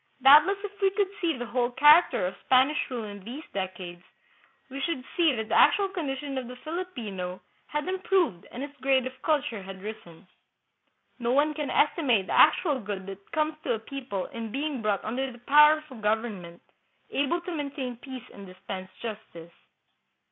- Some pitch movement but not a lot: No, wide, 6.1 semitones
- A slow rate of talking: No, average, 185 wpm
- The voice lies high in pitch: Yes, very high, 260 Hz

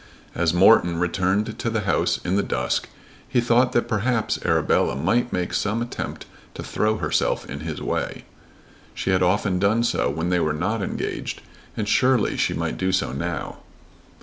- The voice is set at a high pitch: No, low, 100 Hz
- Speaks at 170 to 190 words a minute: Yes, average, 175 wpm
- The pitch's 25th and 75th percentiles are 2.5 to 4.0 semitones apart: No, average, 4.4 semitones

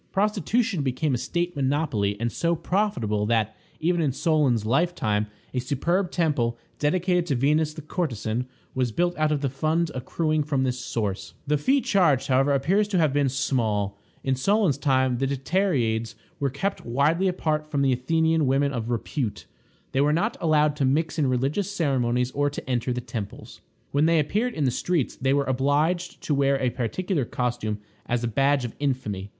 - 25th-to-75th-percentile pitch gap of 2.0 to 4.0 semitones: No, average, 4.7 semitones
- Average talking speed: Yes, average, 180 wpm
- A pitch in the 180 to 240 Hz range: No, medium, 140 Hz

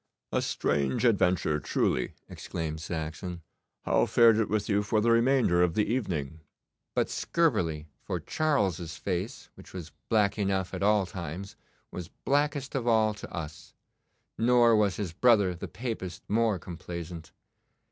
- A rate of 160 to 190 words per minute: No, average, 145 wpm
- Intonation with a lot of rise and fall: No, average, 5.0 semitones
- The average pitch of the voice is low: Yes, low, 100 Hz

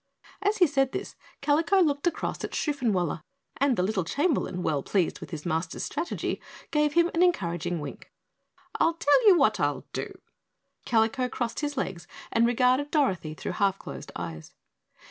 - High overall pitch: Yes, very high, 250 Hz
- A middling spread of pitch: No, wide, 9.0 semitones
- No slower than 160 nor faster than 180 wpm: Yes, average, 165 wpm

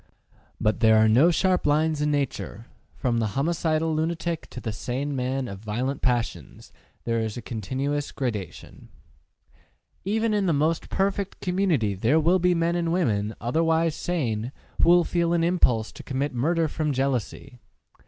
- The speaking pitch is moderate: Yes, medium, 145 Hz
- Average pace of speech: Yes, average, 160 wpm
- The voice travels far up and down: Yes, wide, 6.1 semitones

